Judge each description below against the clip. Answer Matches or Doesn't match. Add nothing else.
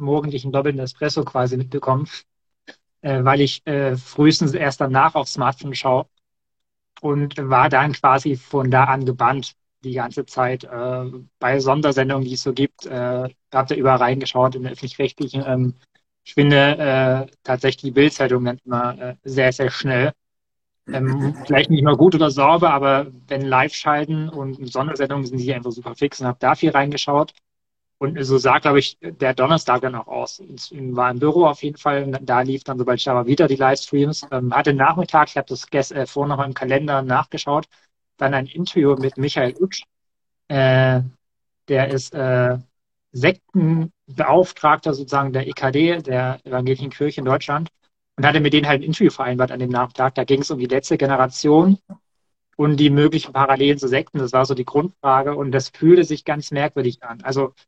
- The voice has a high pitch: Doesn't match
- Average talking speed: Matches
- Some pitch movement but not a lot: Doesn't match